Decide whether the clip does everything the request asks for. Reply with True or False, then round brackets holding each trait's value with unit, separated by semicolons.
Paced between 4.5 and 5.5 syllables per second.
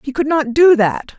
True (4.6 syllables/s)